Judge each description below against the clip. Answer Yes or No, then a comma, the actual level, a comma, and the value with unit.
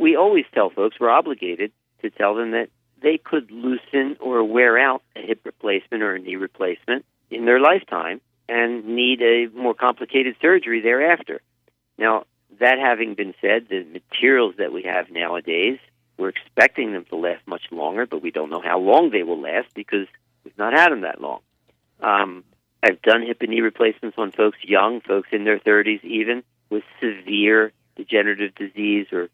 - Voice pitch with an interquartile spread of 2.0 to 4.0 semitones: Yes, average, 3.0 semitones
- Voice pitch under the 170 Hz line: Yes, low, 115 Hz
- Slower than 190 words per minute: Yes, average, 180 wpm